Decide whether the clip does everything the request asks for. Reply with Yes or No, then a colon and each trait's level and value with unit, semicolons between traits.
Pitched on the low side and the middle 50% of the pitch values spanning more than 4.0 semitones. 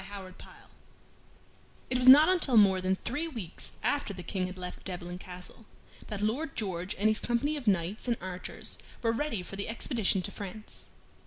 No: high, 205 Hz; average, 4.5 semitones